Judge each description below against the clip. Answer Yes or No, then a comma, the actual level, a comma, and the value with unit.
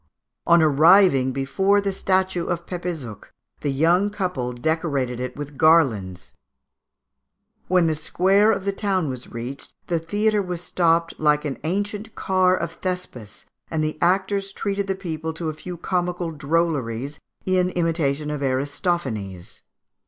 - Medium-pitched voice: Yes, medium, 165 Hz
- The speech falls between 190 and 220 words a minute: No, average, 140 wpm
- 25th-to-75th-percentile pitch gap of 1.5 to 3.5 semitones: No, average, 4.8 semitones